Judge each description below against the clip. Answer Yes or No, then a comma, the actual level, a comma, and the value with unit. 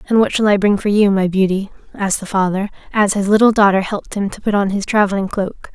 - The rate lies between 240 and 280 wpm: Yes, fast, 250 wpm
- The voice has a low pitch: No, high, 200 Hz